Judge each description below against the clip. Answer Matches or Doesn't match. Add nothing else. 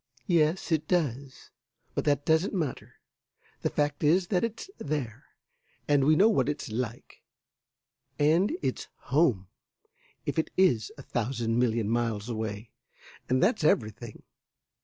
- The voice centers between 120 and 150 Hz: Matches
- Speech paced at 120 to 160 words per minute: Matches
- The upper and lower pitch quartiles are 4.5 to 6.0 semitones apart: Matches